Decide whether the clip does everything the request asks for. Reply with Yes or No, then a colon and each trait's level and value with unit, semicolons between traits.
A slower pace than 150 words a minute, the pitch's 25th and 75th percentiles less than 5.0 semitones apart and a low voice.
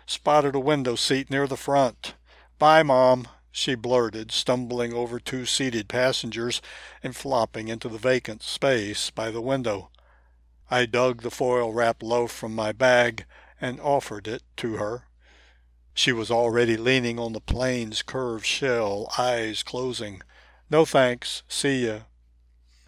Yes: average, 140 wpm; average, 2.7 semitones; low, 120 Hz